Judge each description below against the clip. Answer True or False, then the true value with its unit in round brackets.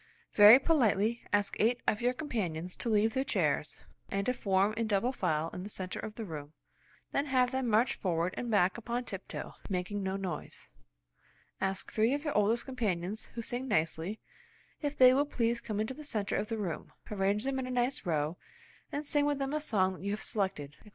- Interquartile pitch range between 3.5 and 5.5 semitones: True (4.7 semitones)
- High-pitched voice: True (215 Hz)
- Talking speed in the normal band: False (210 wpm)